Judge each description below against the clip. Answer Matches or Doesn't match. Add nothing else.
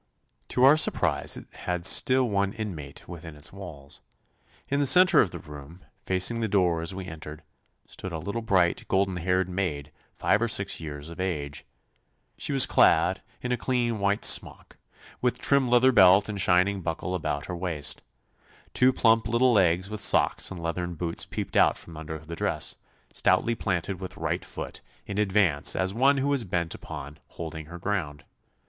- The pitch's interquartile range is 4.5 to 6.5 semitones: Matches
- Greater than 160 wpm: Matches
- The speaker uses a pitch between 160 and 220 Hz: Doesn't match